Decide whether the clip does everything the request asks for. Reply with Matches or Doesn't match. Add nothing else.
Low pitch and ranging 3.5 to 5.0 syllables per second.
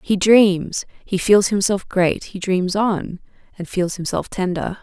Doesn't match